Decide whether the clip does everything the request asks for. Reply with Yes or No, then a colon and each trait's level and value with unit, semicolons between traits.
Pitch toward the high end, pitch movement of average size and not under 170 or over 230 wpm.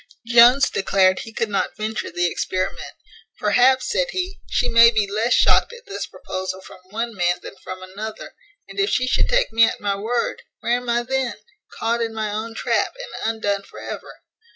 Yes: high, 225 Hz; average, 3.6 semitones; average, 195 wpm